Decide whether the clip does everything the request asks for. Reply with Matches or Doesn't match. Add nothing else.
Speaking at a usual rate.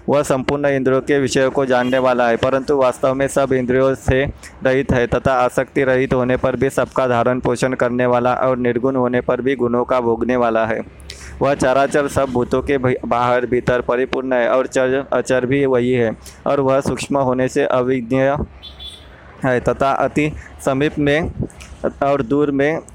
Matches